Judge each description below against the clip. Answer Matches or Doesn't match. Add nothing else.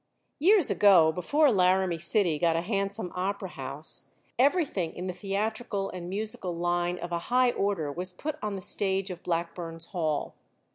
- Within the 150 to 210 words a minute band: Matches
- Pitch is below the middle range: Doesn't match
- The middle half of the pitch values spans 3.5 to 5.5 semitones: Doesn't match